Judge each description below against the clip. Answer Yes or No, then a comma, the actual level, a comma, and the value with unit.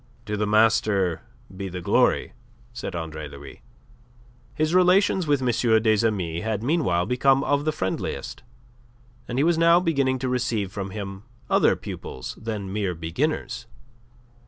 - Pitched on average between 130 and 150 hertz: No, low, 110 Hz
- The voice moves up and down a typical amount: No, wide, 6.3 semitones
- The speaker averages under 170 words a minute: Yes, average, 145 wpm